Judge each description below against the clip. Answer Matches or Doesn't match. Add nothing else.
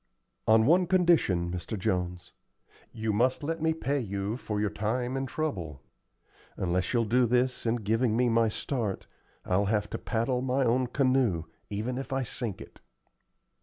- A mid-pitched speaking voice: Doesn't match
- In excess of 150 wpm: Matches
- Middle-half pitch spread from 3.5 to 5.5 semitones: Matches